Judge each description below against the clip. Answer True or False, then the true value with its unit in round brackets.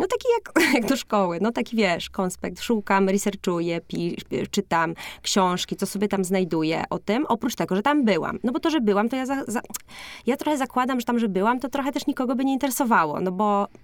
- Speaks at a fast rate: True (220 wpm)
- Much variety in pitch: True (5.7 semitones)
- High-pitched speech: True (225 Hz)